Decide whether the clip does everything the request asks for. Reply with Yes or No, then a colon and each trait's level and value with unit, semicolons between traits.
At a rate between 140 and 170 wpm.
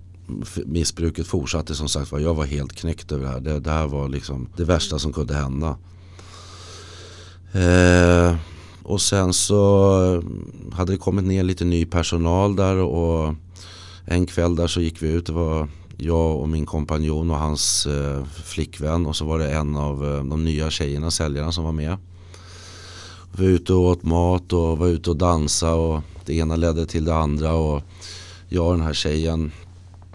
No: average, 180 wpm